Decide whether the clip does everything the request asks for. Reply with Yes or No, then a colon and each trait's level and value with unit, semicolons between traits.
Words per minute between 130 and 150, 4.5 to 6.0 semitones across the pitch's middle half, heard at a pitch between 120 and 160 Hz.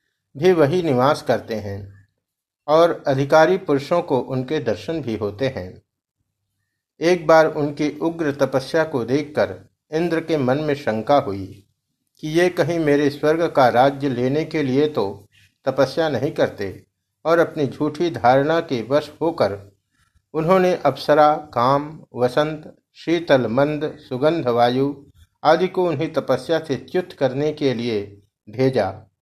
Yes: average, 135 wpm; average, 5.1 semitones; medium, 140 Hz